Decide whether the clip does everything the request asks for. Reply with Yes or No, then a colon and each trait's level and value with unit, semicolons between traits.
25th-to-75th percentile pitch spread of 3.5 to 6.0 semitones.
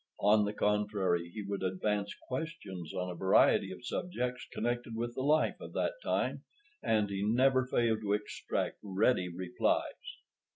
Yes: average, 4.1 semitones